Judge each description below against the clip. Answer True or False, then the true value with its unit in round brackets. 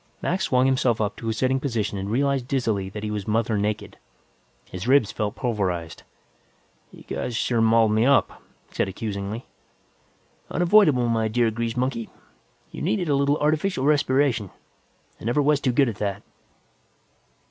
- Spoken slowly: False (160 wpm)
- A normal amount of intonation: True (4.2 semitones)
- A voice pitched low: True (115 Hz)